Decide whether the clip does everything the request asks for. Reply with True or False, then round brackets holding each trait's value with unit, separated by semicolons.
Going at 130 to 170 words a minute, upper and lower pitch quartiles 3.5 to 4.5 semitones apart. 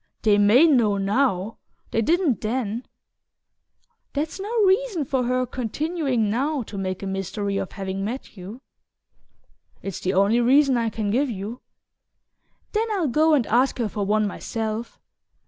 False (155 wpm; 5.3 semitones)